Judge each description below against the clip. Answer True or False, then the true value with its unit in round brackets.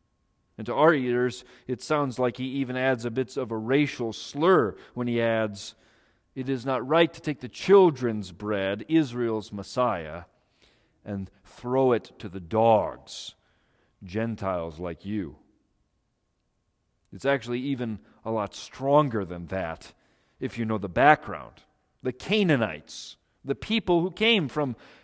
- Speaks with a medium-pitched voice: False (120 Hz)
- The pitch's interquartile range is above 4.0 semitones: True (4.5 semitones)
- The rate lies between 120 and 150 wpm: True (140 wpm)